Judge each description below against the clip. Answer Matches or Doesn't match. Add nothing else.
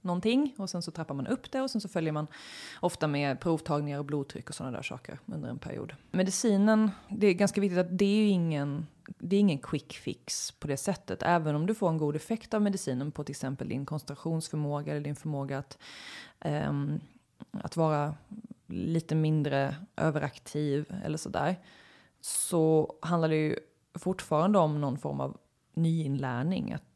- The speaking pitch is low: Doesn't match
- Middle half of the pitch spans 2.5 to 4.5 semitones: Doesn't match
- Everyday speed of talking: Matches